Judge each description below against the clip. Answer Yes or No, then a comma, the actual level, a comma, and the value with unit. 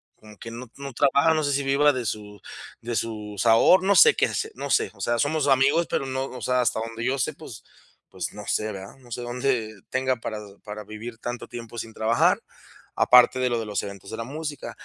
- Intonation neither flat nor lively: Yes, average, 3.7 semitones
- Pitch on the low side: Yes, low, 120 Hz